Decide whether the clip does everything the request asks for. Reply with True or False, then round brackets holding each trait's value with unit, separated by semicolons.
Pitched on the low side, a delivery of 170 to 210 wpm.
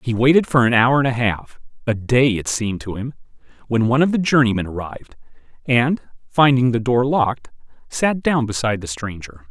True (120 Hz; 185 wpm)